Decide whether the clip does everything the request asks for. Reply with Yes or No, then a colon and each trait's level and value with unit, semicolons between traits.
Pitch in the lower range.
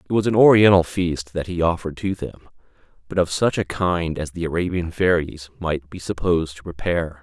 Yes: very low, 85 Hz